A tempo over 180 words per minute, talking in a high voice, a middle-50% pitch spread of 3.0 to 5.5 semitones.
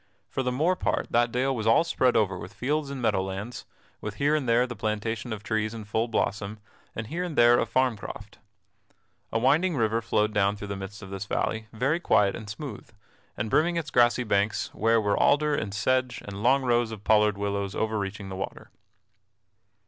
No: average, 200 wpm; low, 110 Hz; average, 3.8 semitones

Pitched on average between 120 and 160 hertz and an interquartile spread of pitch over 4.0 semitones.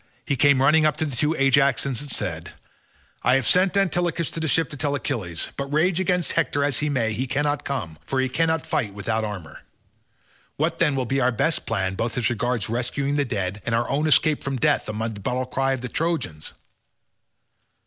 Yes: low, 135 Hz; average, 4.4 semitones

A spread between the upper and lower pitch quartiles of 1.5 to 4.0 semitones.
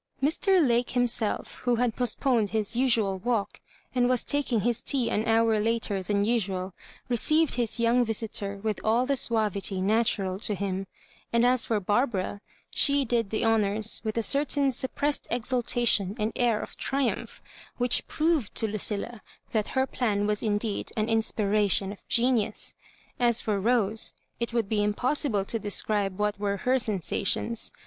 Yes: average, 3.0 semitones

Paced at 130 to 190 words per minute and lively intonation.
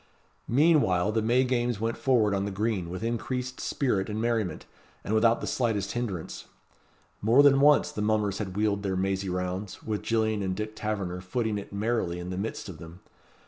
No: average, 185 wpm; average, 3.5 semitones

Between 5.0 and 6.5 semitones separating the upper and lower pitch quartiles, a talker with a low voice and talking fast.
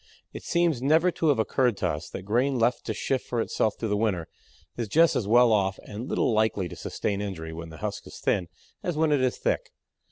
Yes: average, 5.3 semitones; low, 115 Hz; fast, 230 wpm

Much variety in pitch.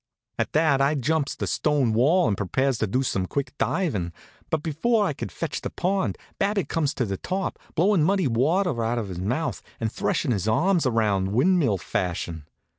Yes: wide, 7.1 semitones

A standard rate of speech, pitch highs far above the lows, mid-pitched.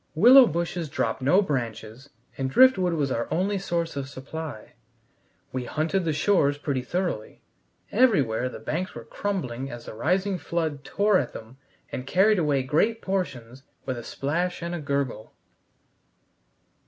Yes: average, 150 wpm; wide, 5.9 semitones; medium, 155 Hz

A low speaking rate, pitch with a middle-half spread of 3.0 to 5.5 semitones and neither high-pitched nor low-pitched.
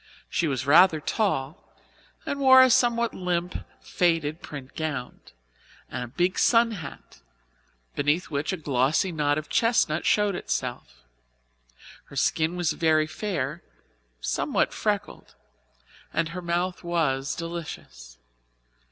Yes: slow, 115 wpm; average, 4.1 semitones; medium, 165 Hz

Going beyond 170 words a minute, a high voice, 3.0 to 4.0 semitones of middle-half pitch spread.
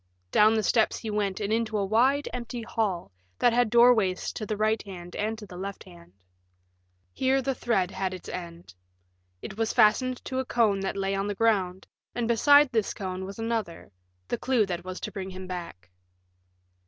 Yes: average, 190 wpm; high, 210 Hz; average, 3.7 semitones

